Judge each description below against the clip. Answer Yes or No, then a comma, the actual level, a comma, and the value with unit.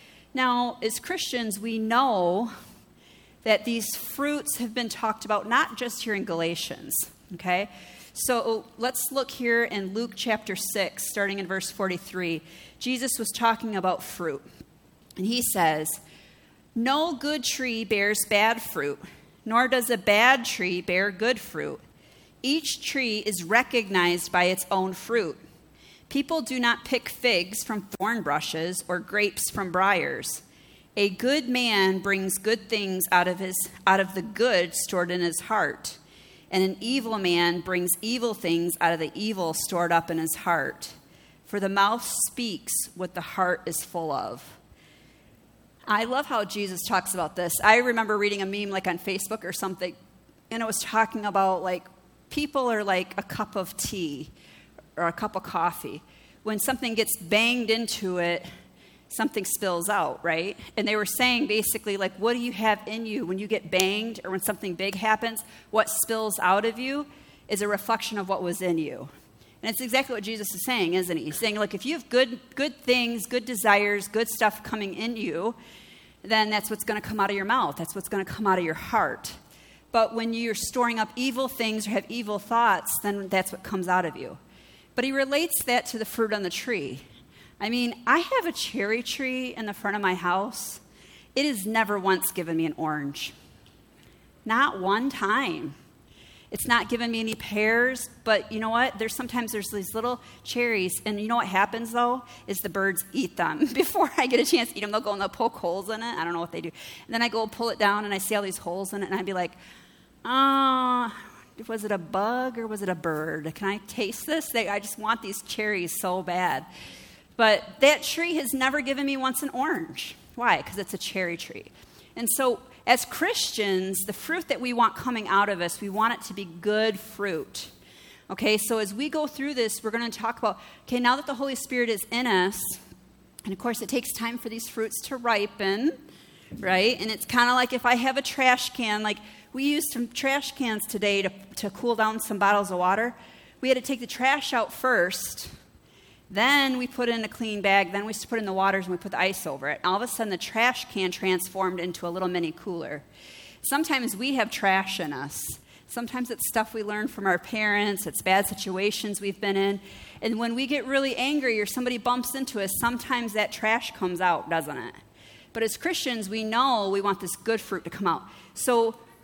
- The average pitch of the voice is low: No, high, 215 Hz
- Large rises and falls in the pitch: No, average, 4.0 semitones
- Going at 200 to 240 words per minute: Yes, fast, 205 wpm